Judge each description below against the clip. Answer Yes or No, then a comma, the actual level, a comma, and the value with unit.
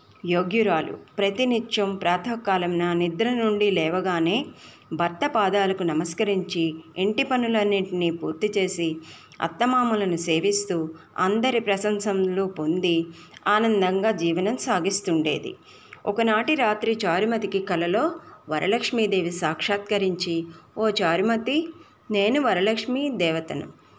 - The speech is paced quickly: No, average, 85 wpm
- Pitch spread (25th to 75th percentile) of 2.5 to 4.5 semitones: Yes, average, 4.2 semitones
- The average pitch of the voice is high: Yes, high, 195 Hz